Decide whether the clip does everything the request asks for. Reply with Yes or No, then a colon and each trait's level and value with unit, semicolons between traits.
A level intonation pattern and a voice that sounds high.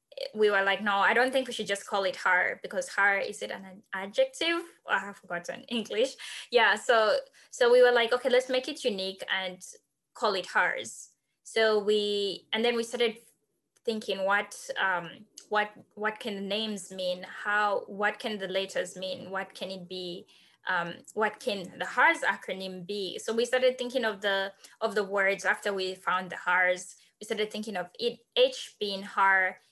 No: average, 3.9 semitones; high, 210 Hz